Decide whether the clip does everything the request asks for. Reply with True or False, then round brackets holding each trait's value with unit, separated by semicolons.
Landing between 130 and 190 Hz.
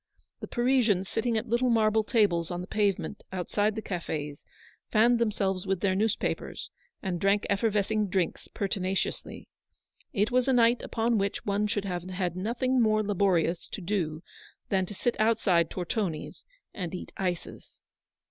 False (200 Hz)